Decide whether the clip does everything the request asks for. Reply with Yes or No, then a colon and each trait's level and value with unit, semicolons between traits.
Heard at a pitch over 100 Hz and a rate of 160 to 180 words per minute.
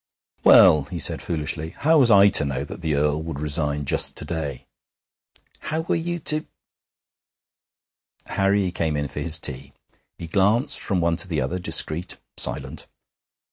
No: very low, 85 Hz; average, 165 wpm